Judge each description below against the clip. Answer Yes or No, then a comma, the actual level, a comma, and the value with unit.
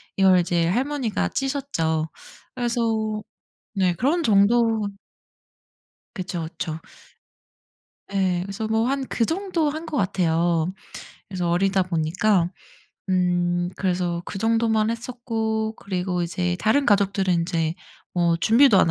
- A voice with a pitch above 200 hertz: No, high, 195 Hz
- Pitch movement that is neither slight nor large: Yes, average, 4.5 semitones